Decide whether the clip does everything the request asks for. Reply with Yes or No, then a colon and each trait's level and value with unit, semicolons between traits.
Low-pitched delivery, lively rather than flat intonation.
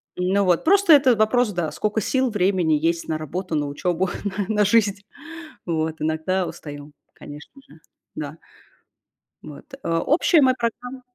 No: medium, 185 Hz; wide, 6.4 semitones